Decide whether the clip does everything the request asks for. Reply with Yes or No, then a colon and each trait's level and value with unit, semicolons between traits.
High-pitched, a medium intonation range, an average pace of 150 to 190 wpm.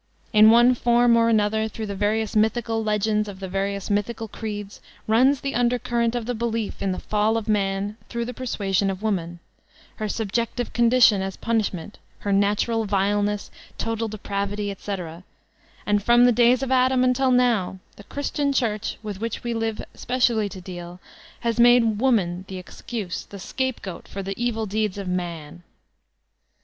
Yes: high, 215 Hz; average, 3.0 semitones; average, 165 wpm